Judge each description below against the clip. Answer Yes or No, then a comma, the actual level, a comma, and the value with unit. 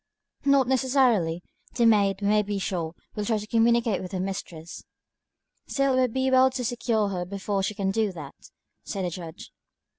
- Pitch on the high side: Yes, high, 210 Hz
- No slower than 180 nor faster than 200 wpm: Yes, average, 185 wpm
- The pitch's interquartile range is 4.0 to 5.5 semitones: Yes, average, 4.3 semitones